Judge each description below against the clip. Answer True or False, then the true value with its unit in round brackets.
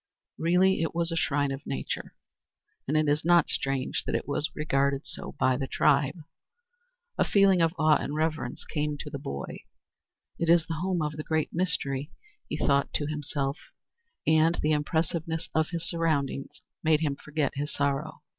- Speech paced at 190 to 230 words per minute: False (175 wpm)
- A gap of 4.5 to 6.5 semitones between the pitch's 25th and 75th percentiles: False (2.5 semitones)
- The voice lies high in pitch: False (155 Hz)